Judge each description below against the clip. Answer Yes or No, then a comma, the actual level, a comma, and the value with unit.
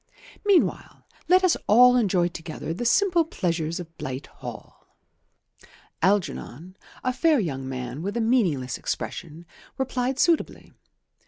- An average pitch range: No, wide, 7.9 semitones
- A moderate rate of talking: No, slow, 120 wpm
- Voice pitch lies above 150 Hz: Yes, high, 190 Hz